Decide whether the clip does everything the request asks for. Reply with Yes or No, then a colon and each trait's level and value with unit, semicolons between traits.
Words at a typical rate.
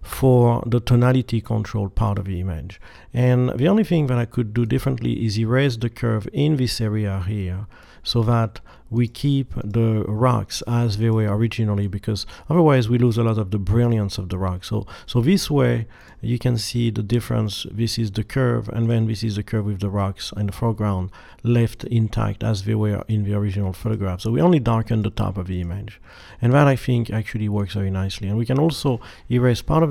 No: fast, 210 wpm